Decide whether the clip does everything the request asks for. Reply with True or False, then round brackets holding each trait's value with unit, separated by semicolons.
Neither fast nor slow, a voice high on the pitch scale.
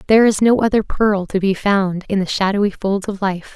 False (235 wpm; 200 Hz)